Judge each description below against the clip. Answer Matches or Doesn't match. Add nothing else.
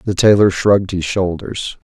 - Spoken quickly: Doesn't match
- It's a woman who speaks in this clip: Doesn't match